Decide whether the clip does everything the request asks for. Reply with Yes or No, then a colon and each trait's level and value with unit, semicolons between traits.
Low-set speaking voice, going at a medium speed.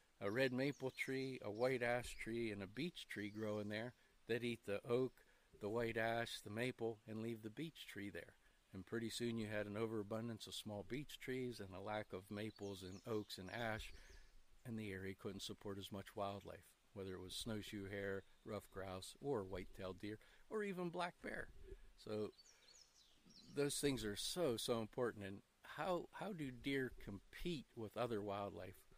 Yes: low, 110 Hz; average, 180 wpm